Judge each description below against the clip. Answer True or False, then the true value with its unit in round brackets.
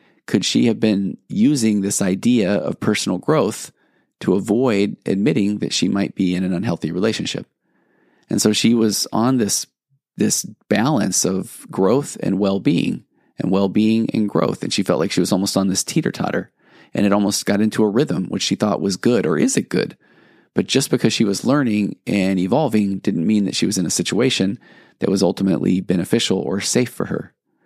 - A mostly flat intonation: True (2.0 semitones)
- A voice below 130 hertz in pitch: True (100 Hz)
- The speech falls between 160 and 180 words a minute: False (190 wpm)